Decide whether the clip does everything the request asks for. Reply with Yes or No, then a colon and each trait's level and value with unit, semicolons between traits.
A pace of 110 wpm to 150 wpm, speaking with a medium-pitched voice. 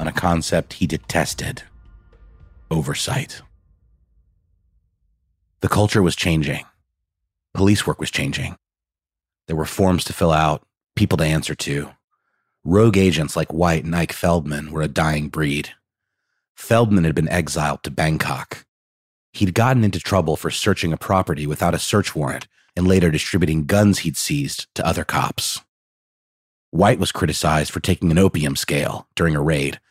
No: average, 145 wpm; very low, 85 Hz